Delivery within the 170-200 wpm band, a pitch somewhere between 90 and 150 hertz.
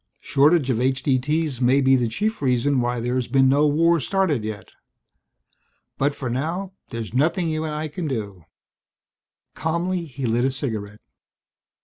No: average, 150 wpm; low, 135 Hz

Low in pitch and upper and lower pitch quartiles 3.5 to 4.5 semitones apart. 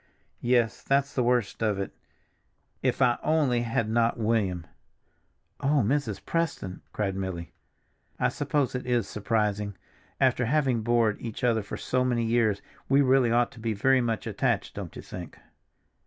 No: low, 120 Hz; average, 3.1 semitones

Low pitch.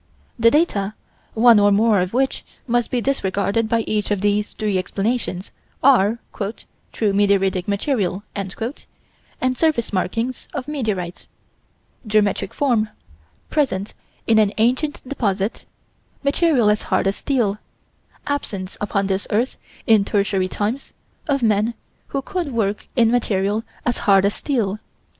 No: high, 215 Hz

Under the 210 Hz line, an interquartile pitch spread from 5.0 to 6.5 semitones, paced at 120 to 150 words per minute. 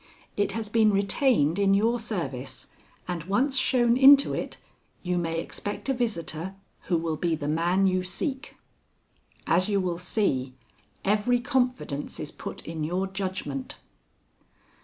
Yes: high, 190 Hz; wide, 5.6 semitones; average, 140 wpm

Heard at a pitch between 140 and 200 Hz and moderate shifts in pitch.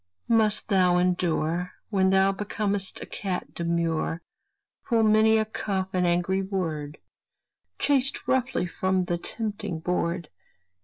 Yes: high, 190 Hz; average, 3.2 semitones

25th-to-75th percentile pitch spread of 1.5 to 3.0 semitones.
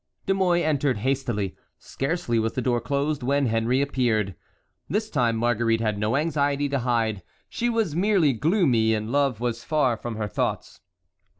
No: average, 4.6 semitones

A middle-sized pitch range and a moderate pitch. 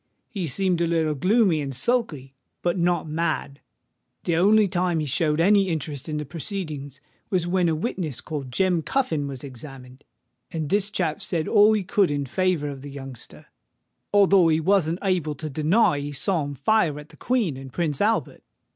Yes: average, 4.7 semitones; medium, 160 Hz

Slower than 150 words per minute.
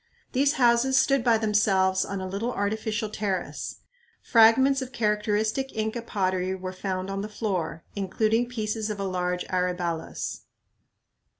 Yes: slow, 135 wpm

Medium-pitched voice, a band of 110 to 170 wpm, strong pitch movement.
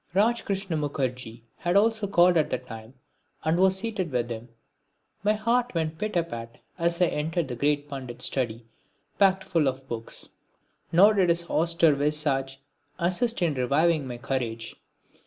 Yes: medium, 160 Hz; average, 155 wpm; wide, 6.1 semitones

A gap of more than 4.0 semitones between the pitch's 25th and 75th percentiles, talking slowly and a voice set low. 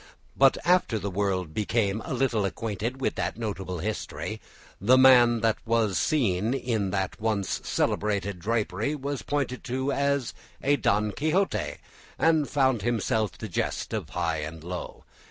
No: average, 5.0 semitones; average, 150 wpm; low, 110 Hz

